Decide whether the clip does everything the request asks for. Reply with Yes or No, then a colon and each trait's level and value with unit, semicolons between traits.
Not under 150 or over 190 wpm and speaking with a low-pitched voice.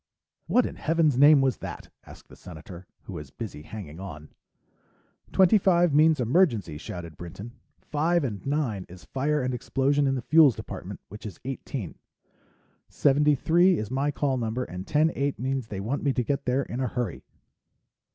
Yes: average, 180 wpm; low, 130 Hz